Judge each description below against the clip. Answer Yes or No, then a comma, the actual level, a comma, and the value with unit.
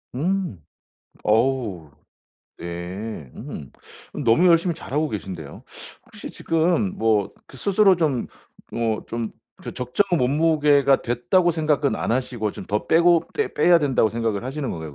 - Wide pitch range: Yes, wide, 7.2 semitones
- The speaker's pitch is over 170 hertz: No, low, 130 Hz